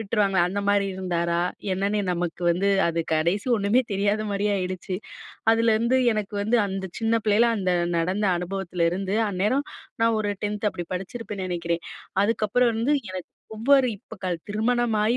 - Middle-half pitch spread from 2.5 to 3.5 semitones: Yes, average, 3.2 semitones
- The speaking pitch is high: Yes, high, 200 Hz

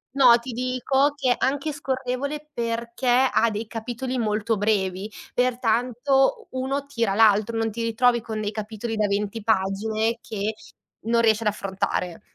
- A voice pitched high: Yes, high, 230 Hz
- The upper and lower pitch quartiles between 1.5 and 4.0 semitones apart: Yes, average, 2.8 semitones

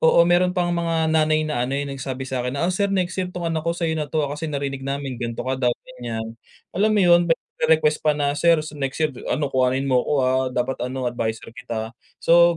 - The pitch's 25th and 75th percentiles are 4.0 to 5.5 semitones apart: Yes, average, 4.4 semitones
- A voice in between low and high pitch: Yes, medium, 145 Hz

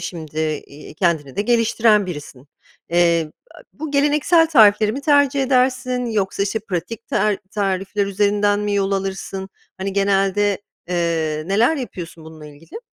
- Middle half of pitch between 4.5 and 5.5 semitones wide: Yes, average, 5.0 semitones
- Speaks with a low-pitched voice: No, high, 200 Hz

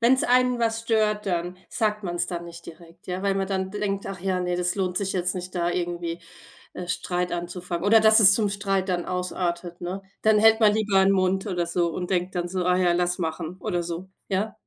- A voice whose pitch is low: No, medium, 185 Hz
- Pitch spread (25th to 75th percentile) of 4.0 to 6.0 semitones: No, narrow, 2.5 semitones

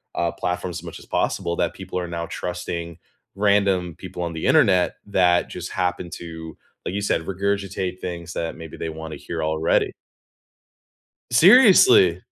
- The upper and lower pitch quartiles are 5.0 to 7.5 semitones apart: No, narrow, 2.5 semitones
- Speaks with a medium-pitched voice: No, very low, 90 Hz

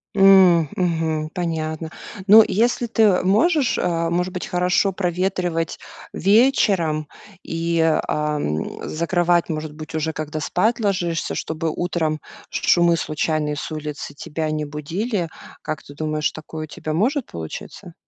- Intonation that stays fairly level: No, average, 3.1 semitones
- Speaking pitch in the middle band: Yes, medium, 165 Hz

